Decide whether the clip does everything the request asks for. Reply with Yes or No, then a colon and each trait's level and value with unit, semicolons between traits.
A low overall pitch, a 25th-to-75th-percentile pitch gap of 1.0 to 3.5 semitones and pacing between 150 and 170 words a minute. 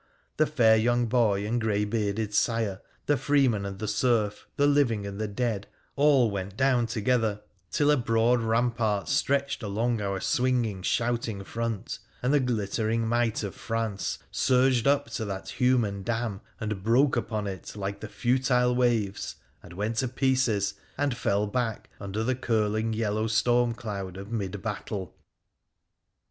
Yes: low, 115 Hz; average, 3.0 semitones; average, 155 wpm